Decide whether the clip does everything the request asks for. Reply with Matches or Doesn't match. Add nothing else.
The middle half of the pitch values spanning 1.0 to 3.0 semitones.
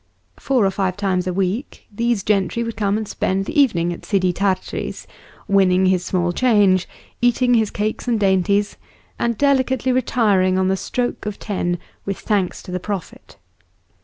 Doesn't match